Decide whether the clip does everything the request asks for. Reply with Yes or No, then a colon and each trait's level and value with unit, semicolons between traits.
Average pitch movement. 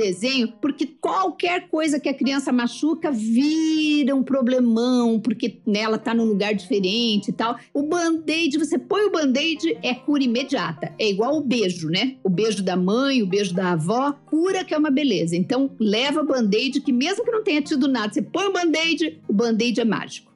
No: wide, 5.7 semitones